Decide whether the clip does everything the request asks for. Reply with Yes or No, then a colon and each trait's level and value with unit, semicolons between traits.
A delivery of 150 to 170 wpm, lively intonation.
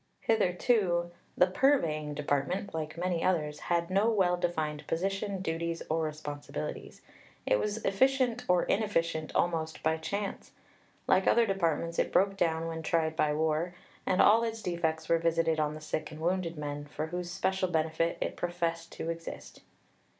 No: average, 155 wpm; average, 3.0 semitones